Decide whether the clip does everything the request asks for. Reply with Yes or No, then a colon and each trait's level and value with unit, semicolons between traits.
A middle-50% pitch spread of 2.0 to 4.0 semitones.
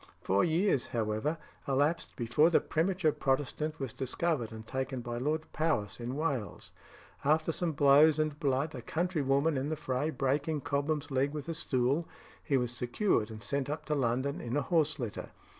Yes: average, 3.6 semitones